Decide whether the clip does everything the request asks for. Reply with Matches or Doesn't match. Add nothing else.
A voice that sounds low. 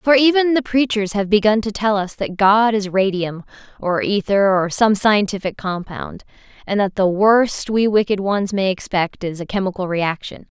Doesn't match